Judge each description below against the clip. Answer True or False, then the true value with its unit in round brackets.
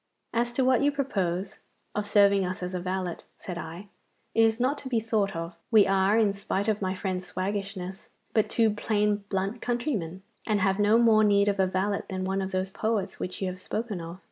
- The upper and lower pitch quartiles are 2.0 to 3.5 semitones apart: True (2.7 semitones)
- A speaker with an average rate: False (215 wpm)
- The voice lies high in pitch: True (200 Hz)